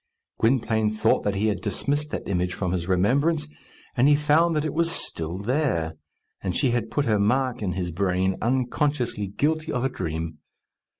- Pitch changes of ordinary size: No, wide, 7.6 semitones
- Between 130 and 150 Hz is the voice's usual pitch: No, low, 110 Hz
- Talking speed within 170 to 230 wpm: Yes, average, 180 wpm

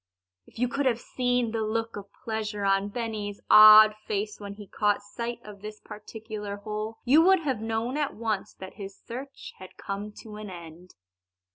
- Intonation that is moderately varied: No, narrow, 2.2 semitones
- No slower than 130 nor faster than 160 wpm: No, average, 180 wpm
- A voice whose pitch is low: No, high, 215 Hz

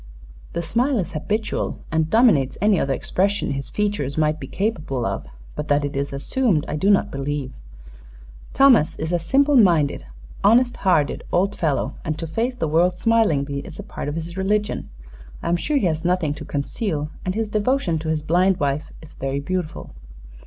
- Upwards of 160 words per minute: Yes, average, 185 wpm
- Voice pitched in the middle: Yes, medium, 170 Hz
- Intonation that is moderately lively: No, wide, 5.8 semitones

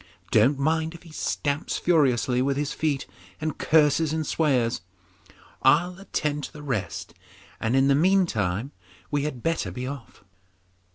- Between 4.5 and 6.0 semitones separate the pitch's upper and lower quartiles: No, average, 3.6 semitones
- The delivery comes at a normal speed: Yes, average, 150 wpm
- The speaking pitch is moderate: Yes, medium, 145 Hz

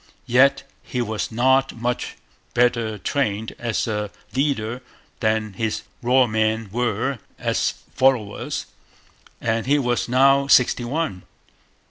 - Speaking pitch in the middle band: No, low, 120 Hz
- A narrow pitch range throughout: No, average, 3.1 semitones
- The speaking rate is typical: No, slow, 115 wpm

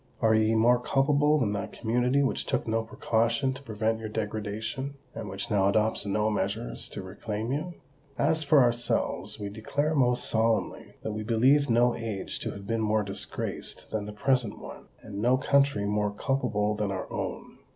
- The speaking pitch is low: Yes, low, 110 Hz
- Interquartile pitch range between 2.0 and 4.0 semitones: Yes, average, 3.6 semitones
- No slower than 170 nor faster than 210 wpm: Yes, average, 180 wpm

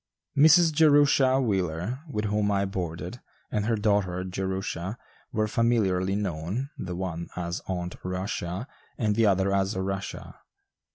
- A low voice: Yes, low, 100 Hz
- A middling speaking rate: No, slow, 130 wpm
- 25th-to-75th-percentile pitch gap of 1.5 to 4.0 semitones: Yes, average, 3.6 semitones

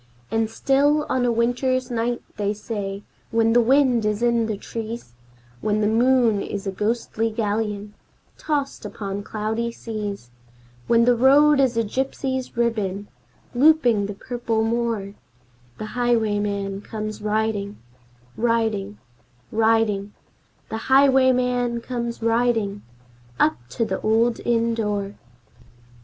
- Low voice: No, high, 225 Hz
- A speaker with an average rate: No, slow, 120 wpm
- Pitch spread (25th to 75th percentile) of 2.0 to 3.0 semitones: Yes, narrow, 2.6 semitones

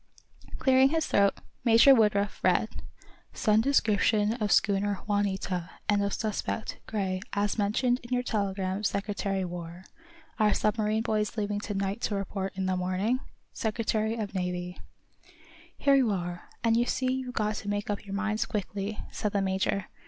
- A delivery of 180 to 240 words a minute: No, average, 155 wpm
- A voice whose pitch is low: No, high, 205 Hz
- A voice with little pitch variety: Yes, narrow, 2.2 semitones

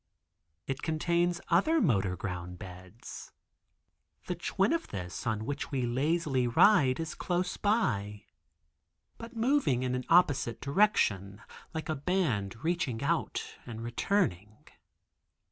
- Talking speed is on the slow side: Yes, slow, 120 wpm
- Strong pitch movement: Yes, wide, 8.4 semitones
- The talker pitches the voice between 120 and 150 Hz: Yes, low, 135 Hz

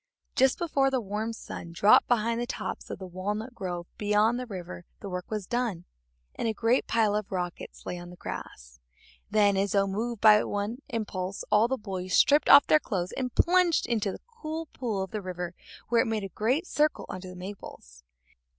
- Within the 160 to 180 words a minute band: No, average, 200 wpm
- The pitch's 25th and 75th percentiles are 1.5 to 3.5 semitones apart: No, average, 4.5 semitones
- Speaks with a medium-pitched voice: No, high, 210 Hz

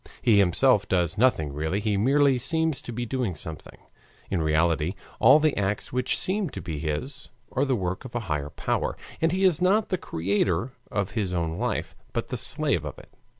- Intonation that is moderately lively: No, wide, 7.8 semitones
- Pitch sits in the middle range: No, low, 105 Hz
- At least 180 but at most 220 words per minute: Yes, average, 195 wpm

